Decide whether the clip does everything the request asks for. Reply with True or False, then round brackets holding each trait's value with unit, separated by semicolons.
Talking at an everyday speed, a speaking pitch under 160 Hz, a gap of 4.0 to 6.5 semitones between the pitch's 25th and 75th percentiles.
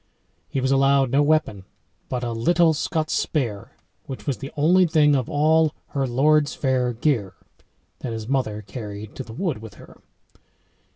True (165 wpm; 135 Hz; 4.8 semitones)